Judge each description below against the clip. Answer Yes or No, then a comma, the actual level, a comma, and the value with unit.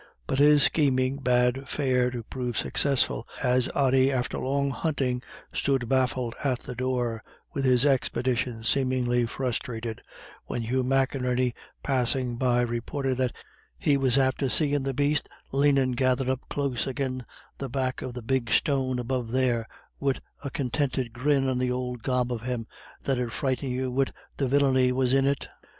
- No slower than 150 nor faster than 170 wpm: Yes, average, 160 wpm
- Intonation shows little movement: Yes, narrow, 1.6 semitones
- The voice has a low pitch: Yes, low, 130 Hz